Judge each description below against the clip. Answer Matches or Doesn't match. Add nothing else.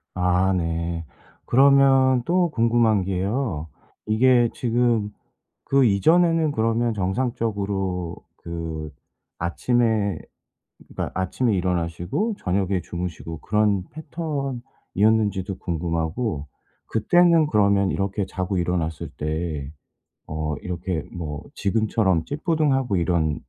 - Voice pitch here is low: Matches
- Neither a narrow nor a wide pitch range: Doesn't match